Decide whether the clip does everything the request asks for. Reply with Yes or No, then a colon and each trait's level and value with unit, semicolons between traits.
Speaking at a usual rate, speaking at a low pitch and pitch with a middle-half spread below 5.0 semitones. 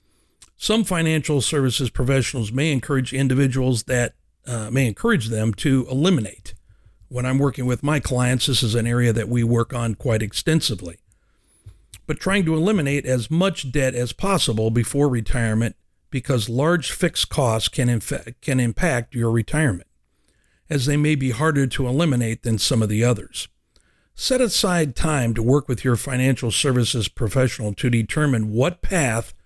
Yes: average, 155 wpm; low, 125 Hz; average, 4.1 semitones